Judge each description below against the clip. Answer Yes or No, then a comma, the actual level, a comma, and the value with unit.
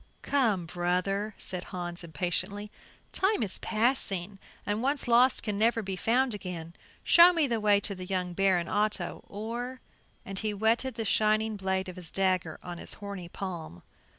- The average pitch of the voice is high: Yes, high, 200 Hz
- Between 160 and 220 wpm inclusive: Yes, average, 170 wpm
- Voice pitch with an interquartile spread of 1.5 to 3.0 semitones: No, average, 3.6 semitones